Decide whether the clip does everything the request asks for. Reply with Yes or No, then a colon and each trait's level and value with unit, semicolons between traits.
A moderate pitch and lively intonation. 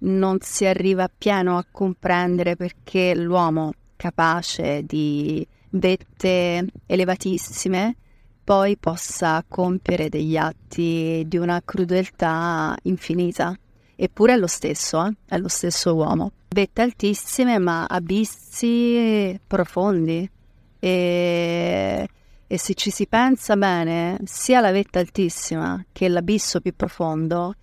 No: medium, 180 Hz; narrow, 2.5 semitones